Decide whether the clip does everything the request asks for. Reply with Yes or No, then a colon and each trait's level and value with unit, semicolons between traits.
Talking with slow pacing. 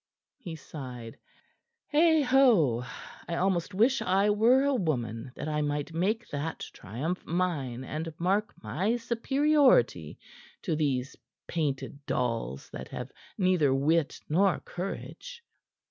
Yes: slow, 115 wpm